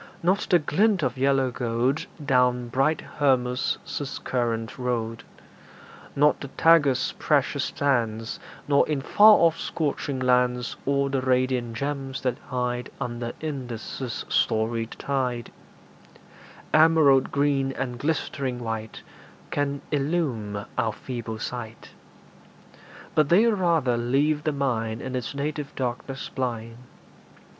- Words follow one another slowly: Yes, slow, 115 wpm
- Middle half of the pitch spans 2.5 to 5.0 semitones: Yes, average, 3.1 semitones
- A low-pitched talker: Yes, low, 130 Hz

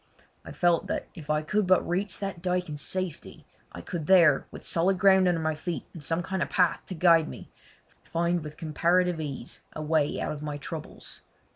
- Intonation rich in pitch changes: No, average, 2.9 semitones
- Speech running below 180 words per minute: No, fast, 205 wpm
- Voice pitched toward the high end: No, medium, 170 Hz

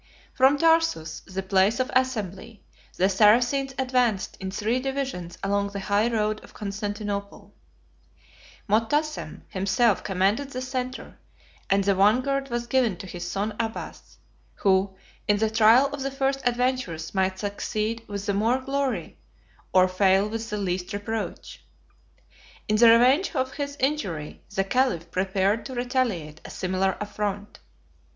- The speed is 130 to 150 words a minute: Yes, average, 140 wpm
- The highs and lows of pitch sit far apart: No, average, 4.8 semitones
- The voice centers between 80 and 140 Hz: No, high, 215 Hz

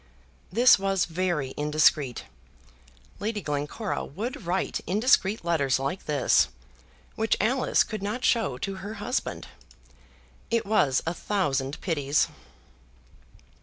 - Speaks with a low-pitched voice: No, medium, 185 Hz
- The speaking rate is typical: No, slow, 110 wpm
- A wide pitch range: Yes, wide, 6.4 semitones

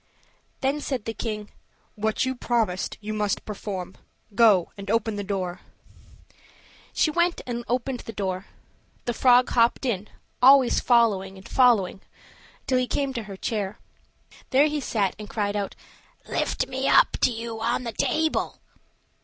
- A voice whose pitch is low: No, high, 225 Hz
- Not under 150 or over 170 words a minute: Yes, average, 160 wpm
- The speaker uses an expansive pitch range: No, average, 3.8 semitones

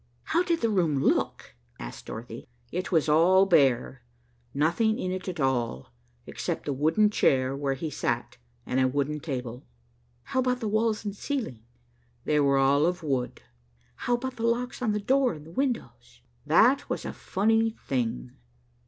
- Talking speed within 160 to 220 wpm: Yes, average, 165 wpm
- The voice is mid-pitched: Yes, medium, 165 Hz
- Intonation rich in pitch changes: Yes, wide, 8.7 semitones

